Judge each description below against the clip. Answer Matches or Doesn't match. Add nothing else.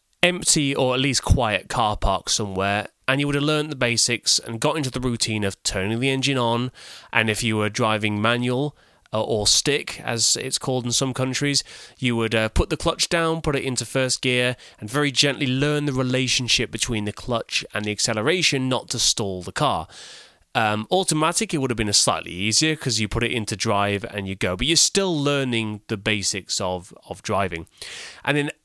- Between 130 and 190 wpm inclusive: Doesn't match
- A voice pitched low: Matches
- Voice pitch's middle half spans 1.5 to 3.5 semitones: Doesn't match